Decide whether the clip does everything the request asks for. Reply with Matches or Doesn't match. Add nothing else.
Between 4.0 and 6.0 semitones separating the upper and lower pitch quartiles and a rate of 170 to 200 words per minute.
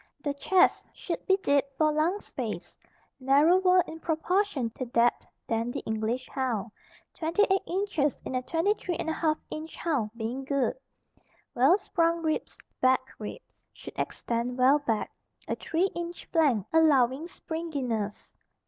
Doesn't match